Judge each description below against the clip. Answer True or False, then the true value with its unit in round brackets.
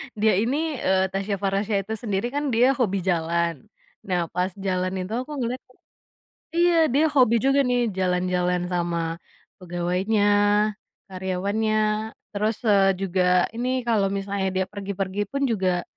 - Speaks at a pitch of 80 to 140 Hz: False (195 Hz)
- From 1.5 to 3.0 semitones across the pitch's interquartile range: False (4.4 semitones)